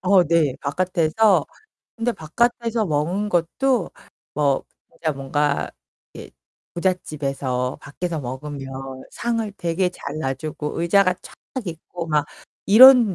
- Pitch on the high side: No, medium, 170 Hz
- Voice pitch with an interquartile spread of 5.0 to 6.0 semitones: Yes, average, 5.3 semitones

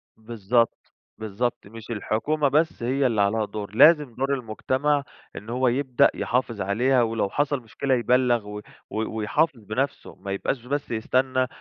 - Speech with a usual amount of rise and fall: Yes, average, 3.5 semitones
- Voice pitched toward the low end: Yes, low, 120 Hz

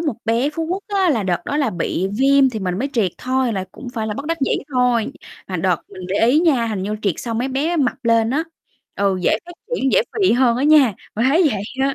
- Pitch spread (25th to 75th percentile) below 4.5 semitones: No, average, 5.2 semitones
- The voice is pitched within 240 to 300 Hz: Yes, very high, 250 Hz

